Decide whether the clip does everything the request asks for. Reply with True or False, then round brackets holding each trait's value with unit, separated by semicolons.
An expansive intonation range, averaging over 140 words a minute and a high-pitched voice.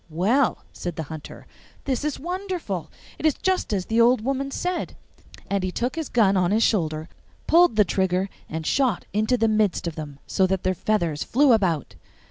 True (6.8 semitones; 190 wpm; 210 Hz)